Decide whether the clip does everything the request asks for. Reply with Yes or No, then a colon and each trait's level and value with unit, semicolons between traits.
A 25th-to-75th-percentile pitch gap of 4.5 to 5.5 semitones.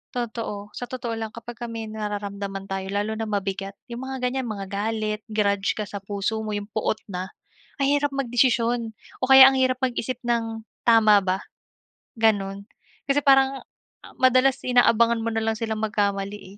No: average, 3.2 semitones